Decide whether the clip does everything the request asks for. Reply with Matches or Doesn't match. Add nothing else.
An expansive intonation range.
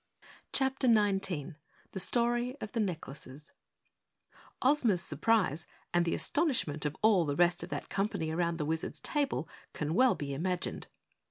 Matches